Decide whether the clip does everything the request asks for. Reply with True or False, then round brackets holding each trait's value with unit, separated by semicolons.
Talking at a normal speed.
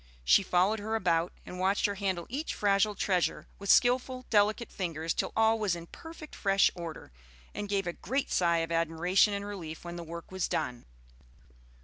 True (185 wpm)